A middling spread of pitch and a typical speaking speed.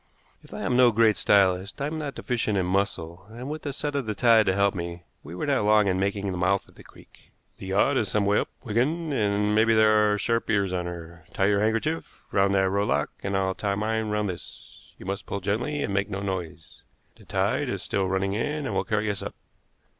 No: average, 3.0 semitones; fast, 235 wpm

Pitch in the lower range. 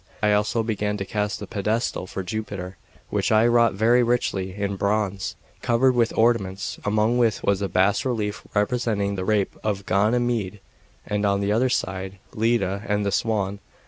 Yes: low, 105 Hz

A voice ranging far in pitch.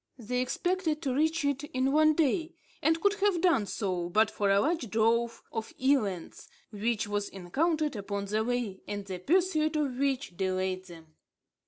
Yes: wide, 7.3 semitones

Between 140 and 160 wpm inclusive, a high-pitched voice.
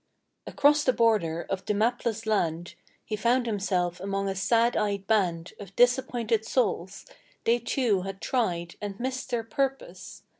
Yes: average, 150 wpm; high, 215 Hz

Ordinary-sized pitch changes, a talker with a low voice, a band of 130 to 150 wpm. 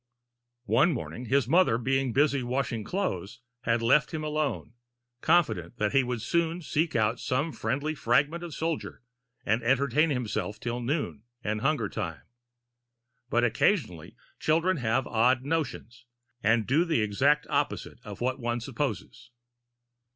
Yes: average, 4.8 semitones; low, 130 Hz; average, 140 wpm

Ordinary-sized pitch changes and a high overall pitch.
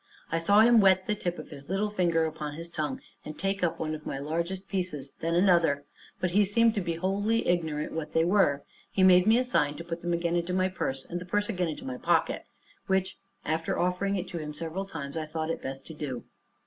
No: average, 3.5 semitones; medium, 170 Hz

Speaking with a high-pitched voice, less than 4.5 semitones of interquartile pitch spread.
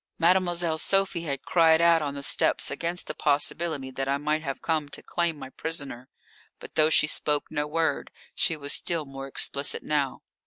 No: medium, 155 Hz; average, 2.9 semitones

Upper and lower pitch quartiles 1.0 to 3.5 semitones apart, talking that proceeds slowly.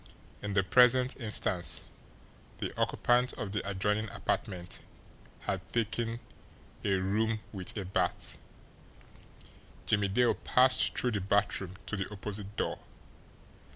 Yes: average, 2.9 semitones; slow, 120 wpm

